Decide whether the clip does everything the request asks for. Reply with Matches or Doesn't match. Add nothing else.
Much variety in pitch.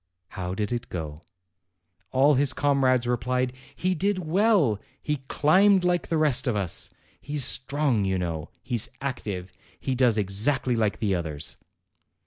Matches